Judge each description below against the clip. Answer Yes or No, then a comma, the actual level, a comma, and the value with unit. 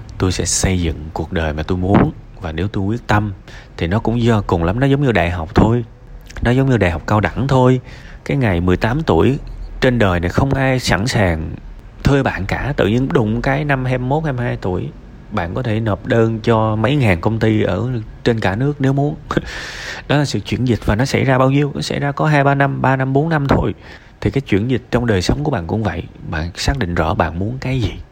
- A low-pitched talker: Yes, low, 115 Hz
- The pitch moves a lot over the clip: Yes, wide, 5.7 semitones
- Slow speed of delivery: No, average, 245 wpm